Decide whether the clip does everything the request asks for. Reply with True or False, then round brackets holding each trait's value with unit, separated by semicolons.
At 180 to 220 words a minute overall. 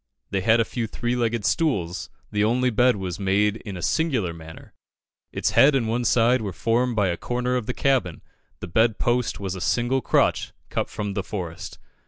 True (200 wpm)